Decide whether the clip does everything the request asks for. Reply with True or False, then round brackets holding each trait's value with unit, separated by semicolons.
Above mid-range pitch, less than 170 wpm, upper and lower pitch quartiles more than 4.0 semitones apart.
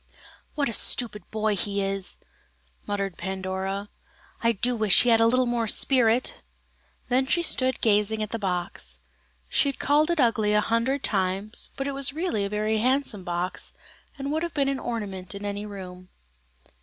False (215 Hz; 175 wpm; 4.5 semitones)